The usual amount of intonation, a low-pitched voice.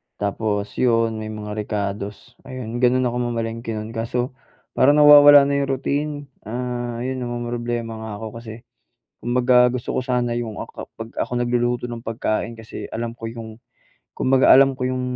No: narrow, 1.9 semitones; low, 120 Hz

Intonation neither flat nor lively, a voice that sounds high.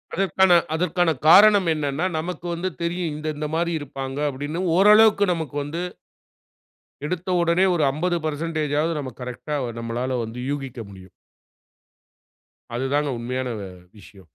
No: average, 4.7 semitones; medium, 155 Hz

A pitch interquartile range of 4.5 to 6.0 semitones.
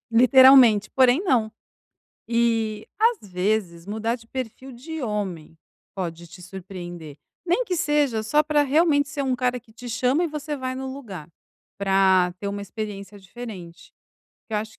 Yes: wide, 5.4 semitones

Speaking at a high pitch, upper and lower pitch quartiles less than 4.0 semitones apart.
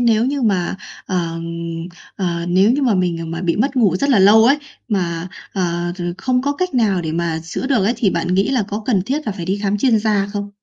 No: high, 200 Hz; average, 5.3 semitones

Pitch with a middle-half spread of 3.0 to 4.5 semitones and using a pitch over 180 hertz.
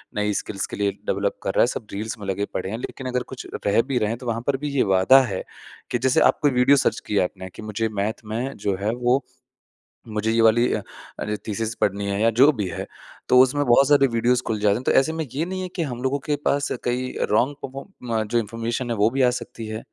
No: average, 3.9 semitones; low, 115 Hz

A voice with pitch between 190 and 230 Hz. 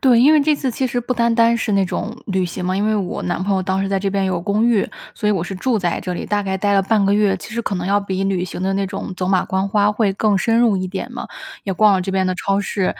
Yes: high, 200 Hz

